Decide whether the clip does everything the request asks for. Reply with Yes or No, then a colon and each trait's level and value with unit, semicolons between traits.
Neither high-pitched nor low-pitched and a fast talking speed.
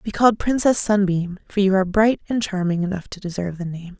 No: high, 195 Hz; fast, 225 wpm